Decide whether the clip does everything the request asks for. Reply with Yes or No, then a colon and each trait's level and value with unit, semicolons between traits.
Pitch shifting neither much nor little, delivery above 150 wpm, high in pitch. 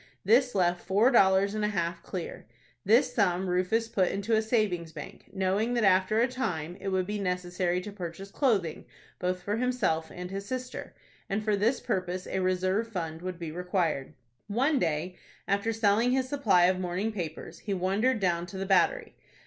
Yes: average, 3.6 semitones; average, 180 wpm; high, 195 Hz